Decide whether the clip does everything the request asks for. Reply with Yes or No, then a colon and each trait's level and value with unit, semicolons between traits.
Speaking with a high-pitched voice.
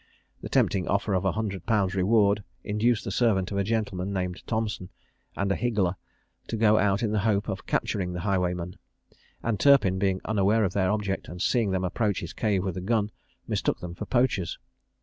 No: low, 100 Hz